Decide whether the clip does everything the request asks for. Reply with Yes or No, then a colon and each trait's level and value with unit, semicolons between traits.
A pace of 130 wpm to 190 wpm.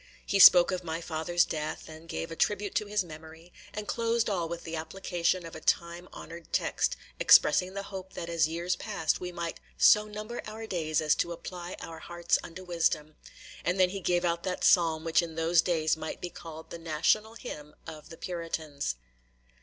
No: average, 200 wpm